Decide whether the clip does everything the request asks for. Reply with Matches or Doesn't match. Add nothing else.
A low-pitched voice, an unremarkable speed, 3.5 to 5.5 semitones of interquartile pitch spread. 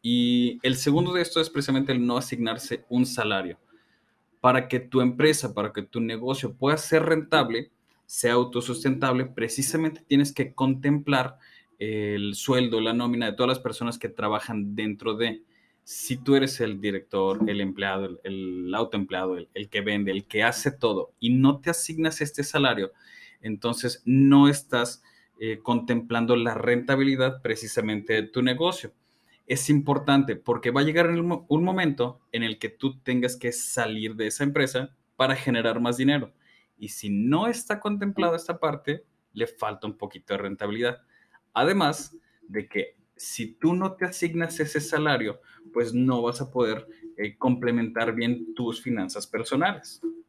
Matches